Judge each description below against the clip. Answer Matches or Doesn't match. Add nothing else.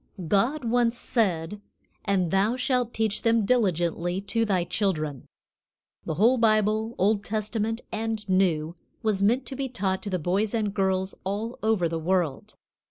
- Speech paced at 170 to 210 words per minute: Doesn't match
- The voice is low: Doesn't match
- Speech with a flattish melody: Doesn't match